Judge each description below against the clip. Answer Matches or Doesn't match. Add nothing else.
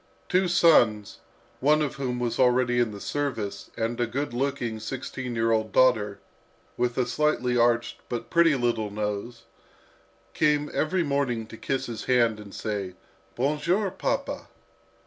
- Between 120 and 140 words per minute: Doesn't match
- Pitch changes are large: Doesn't match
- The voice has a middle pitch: Doesn't match